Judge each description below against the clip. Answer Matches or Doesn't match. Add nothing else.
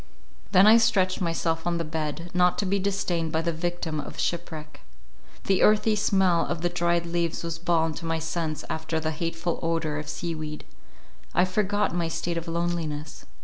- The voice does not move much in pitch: Matches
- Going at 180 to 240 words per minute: Matches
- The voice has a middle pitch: Matches